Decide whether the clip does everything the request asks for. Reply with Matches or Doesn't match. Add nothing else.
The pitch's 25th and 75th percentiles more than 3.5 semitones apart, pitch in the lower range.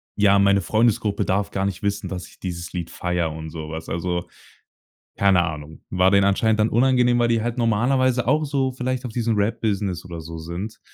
Matches